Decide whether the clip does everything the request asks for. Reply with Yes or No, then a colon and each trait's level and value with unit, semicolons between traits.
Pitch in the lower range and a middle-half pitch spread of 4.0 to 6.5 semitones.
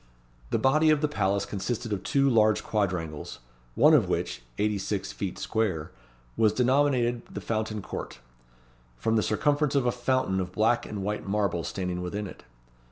Yes: low, 105 Hz; average, 4.3 semitones